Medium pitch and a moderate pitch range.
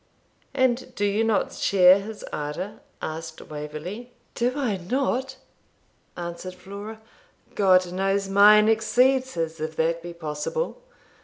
No: high, 195 Hz; average, 5.0 semitones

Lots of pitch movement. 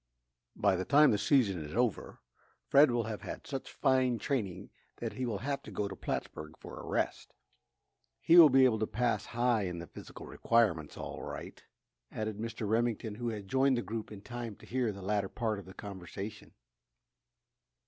No: average, 3.6 semitones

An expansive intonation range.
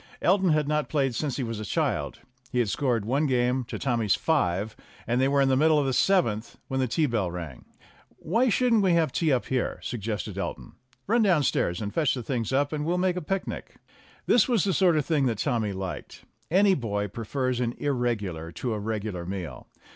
Yes: wide, 6.2 semitones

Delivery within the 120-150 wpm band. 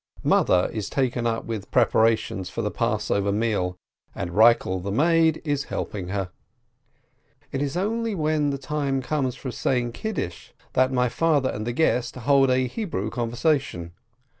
No: average, 160 wpm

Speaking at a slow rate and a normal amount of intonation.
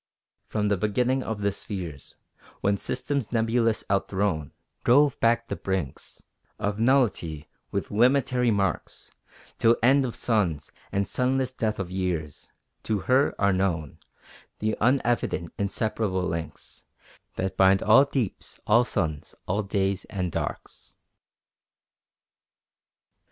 Yes: slow, 120 wpm; average, 4.3 semitones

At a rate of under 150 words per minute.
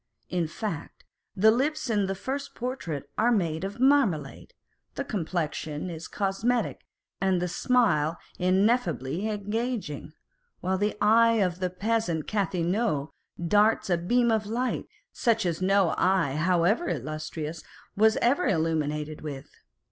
Yes: slow, 135 wpm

